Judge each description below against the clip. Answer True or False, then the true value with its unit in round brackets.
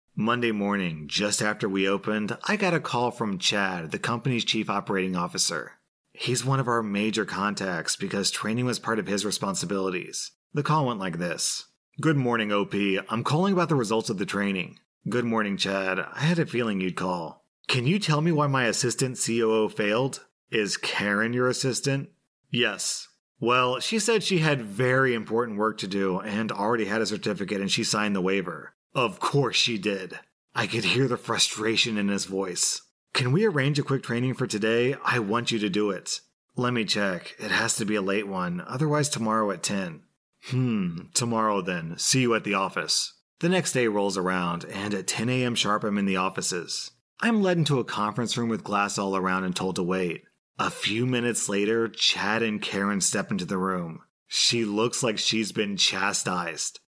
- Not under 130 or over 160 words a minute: False (190 wpm)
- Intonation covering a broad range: False (3.9 semitones)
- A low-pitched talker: True (110 Hz)